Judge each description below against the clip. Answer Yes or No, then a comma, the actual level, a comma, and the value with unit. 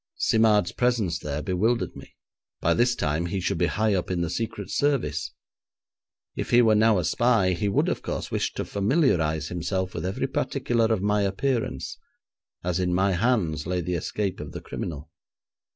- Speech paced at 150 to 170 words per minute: No, average, 180 wpm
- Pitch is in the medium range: No, very low, 95 Hz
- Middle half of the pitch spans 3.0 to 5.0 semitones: Yes, average, 4.6 semitones